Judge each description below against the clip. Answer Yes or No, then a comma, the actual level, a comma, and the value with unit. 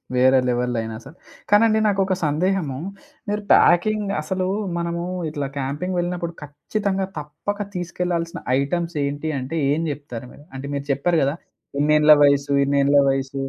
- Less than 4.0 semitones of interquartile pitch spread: No, average, 4.4 semitones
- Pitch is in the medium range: Yes, medium, 155 Hz